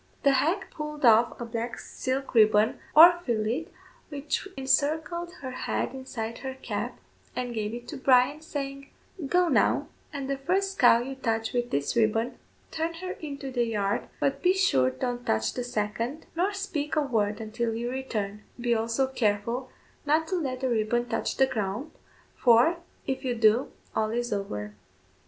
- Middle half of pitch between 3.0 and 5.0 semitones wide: Yes, average, 4.3 semitones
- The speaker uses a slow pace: No, average, 170 wpm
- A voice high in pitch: Yes, very high, 250 Hz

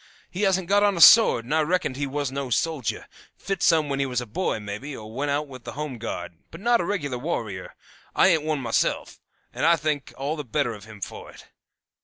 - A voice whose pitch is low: No, medium, 145 Hz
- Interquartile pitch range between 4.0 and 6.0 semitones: Yes, average, 5.1 semitones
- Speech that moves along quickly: Yes, fast, 235 wpm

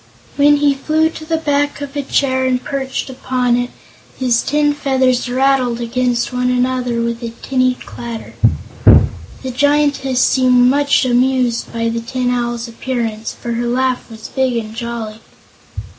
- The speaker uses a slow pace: No, average, 155 wpm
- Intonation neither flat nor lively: No, narrow, 2.2 semitones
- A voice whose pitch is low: No, very high, 255 Hz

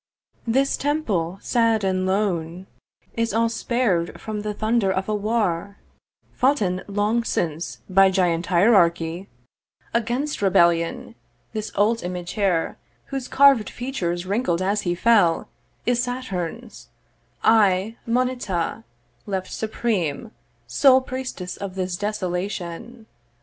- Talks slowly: Yes, slow, 115 wpm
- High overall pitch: Yes, high, 205 Hz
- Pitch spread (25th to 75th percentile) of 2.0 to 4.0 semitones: No, average, 4.5 semitones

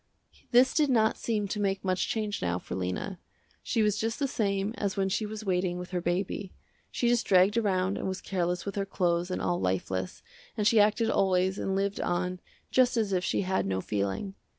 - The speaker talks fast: Yes, fast, 210 wpm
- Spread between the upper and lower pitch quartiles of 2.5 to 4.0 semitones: Yes, average, 2.8 semitones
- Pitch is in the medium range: No, high, 195 Hz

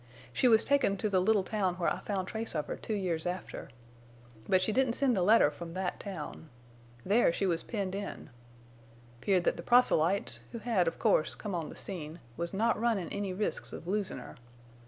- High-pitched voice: Yes, high, 195 Hz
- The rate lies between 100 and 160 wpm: No, average, 200 wpm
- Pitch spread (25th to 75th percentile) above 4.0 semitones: No, average, 3.7 semitones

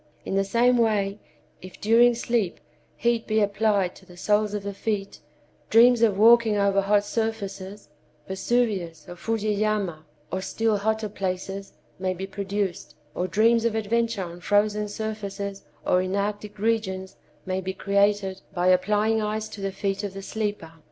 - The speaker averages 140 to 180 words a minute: Yes, average, 150 wpm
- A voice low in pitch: No, high, 205 Hz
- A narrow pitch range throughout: Yes, narrow, 2.3 semitones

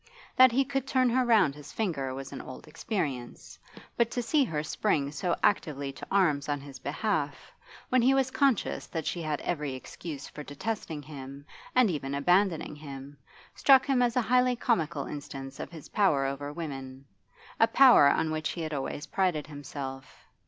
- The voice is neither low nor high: Yes, medium, 155 Hz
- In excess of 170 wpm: Yes, average, 180 wpm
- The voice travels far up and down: Yes, wide, 8.1 semitones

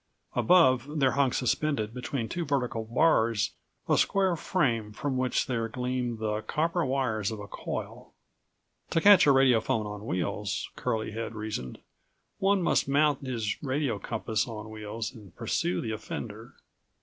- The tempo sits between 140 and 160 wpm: Yes, average, 150 wpm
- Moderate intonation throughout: Yes, average, 4.4 semitones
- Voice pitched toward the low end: Yes, low, 120 Hz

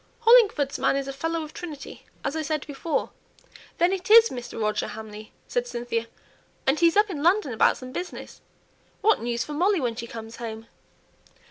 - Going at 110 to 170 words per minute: No, average, 185 wpm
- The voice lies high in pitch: Yes, very high, 280 Hz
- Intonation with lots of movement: Yes, wide, 6.7 semitones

